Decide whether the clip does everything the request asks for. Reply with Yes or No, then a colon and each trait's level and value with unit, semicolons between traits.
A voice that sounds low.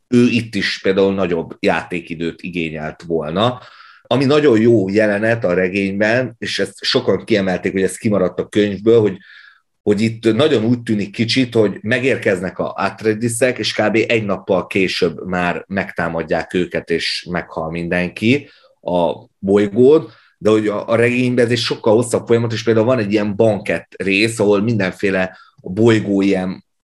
Yes: low, 105 Hz